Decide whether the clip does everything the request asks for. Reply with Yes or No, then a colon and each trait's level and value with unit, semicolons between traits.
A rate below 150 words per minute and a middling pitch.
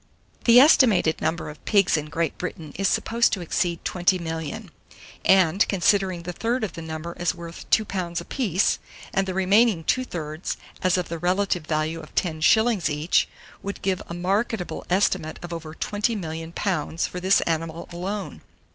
No: average, 165 wpm; medium, 175 Hz